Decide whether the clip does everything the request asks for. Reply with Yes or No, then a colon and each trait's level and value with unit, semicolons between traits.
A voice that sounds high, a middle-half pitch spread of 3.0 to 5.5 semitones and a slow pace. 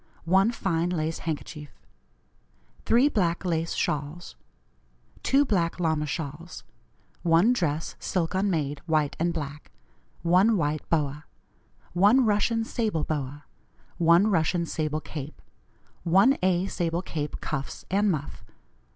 No: medium, 170 Hz; average, 4.0 semitones; slow, 115 wpm